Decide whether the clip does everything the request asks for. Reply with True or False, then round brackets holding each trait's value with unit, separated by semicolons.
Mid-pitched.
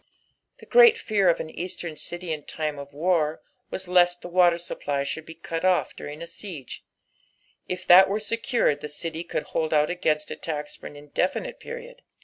True (170 Hz)